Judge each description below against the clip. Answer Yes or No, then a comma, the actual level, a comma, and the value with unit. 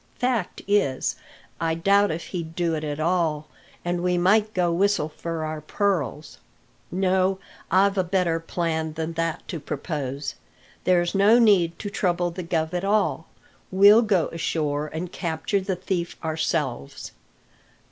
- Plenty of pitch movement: No, average, 3.3 semitones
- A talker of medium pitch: Yes, medium, 175 Hz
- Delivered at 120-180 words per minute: Yes, average, 145 wpm